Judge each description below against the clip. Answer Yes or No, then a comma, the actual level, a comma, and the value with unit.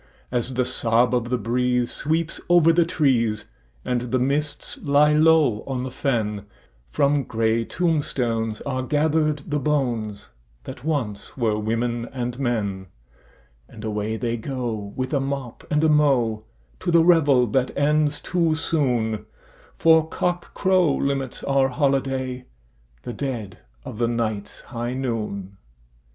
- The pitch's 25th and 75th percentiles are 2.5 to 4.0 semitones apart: No, average, 4.4 semitones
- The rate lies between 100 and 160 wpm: Yes, slow, 135 wpm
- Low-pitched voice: Yes, low, 125 Hz